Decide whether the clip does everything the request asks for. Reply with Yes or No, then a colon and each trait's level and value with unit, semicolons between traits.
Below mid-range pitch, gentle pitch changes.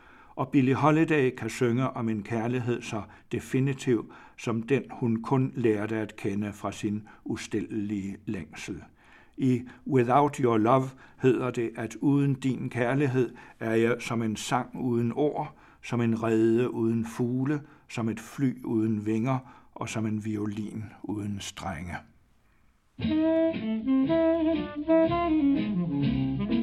No: low, 120 Hz; average, 3.9 semitones